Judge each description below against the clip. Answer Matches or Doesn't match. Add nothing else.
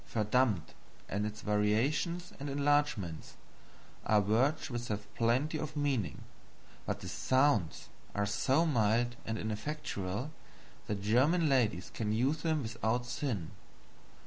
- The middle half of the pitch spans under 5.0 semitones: Doesn't match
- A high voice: Doesn't match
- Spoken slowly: Matches